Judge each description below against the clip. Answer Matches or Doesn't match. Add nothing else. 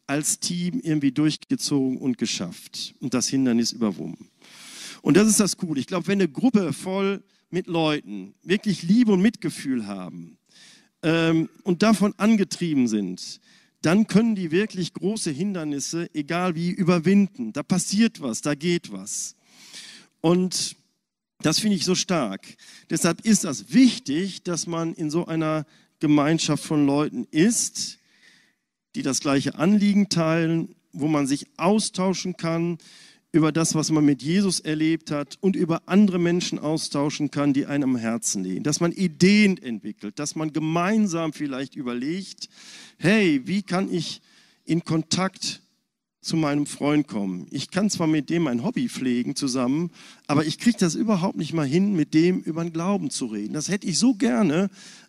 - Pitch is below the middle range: Doesn't match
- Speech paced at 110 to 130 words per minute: Doesn't match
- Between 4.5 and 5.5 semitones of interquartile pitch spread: Matches